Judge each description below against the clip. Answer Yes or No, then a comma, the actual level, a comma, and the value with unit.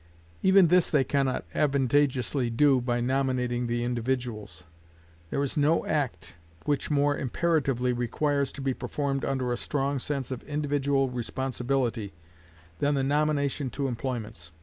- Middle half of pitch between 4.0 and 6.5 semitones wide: No, average, 2.7 semitones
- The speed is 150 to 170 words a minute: No, average, 140 wpm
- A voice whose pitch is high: No, low, 135 Hz